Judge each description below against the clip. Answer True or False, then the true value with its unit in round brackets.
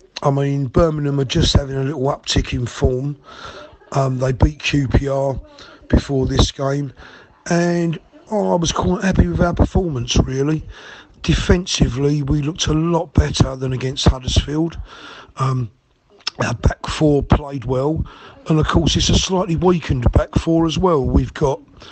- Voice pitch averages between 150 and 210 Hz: False (140 Hz)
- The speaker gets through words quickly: False (155 wpm)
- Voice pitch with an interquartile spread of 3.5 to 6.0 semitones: True (3.9 semitones)